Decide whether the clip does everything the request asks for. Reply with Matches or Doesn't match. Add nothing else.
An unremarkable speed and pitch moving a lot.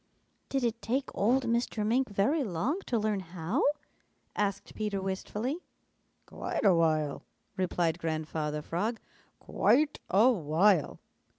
Doesn't match